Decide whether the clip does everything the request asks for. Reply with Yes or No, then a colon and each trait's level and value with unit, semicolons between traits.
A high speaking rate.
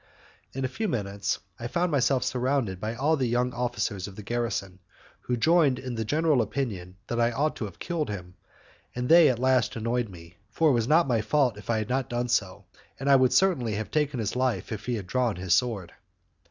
Yes: fast, 220 wpm